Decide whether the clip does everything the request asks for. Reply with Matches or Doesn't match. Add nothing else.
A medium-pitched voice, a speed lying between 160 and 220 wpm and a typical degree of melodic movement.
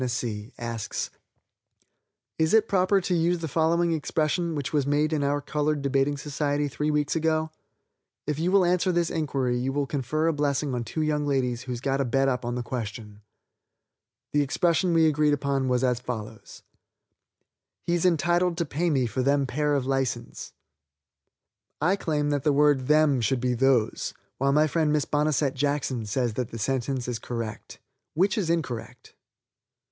Matches